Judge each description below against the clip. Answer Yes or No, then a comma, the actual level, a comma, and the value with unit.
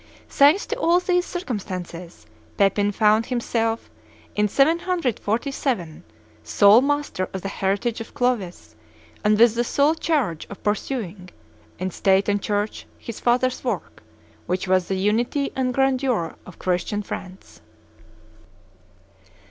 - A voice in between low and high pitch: No, high, 220 Hz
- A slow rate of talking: Yes, slow, 125 wpm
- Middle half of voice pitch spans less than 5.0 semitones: No, wide, 5.6 semitones